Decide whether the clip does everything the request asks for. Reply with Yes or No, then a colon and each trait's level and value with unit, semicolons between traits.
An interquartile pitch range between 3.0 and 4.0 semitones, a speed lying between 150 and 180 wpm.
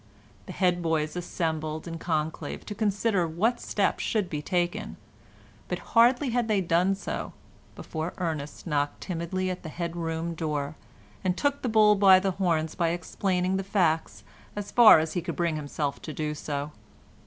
Yes: average, 3.6 semitones; average, 170 wpm